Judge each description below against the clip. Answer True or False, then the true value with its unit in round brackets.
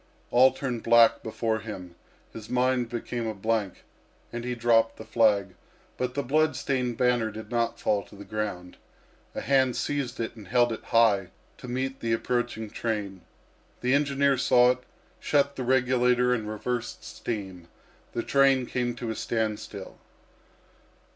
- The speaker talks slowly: False (155 wpm)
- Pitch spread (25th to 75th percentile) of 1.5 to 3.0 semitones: True (2.4 semitones)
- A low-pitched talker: True (120 Hz)